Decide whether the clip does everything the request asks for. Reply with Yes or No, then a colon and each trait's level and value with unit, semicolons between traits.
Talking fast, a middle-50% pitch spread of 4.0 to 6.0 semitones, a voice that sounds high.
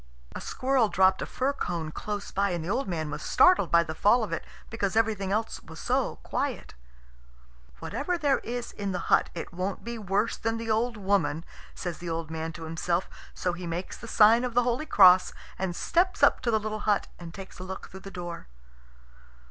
Yes: fast, 210 wpm; average, 4.7 semitones; high, 195 Hz